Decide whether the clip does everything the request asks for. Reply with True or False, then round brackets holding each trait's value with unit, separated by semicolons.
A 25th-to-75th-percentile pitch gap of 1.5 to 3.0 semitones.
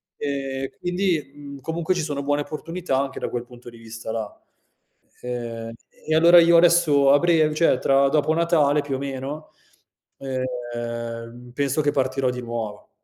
False (4.1 semitones)